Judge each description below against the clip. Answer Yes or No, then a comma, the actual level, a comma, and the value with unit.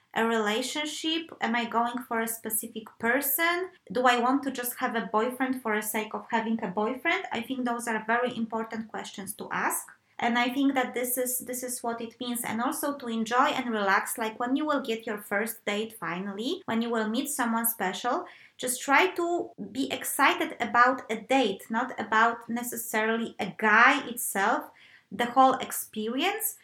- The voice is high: Yes, high, 240 Hz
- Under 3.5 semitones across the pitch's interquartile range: Yes, narrow, 2.6 semitones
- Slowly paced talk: No, average, 185 wpm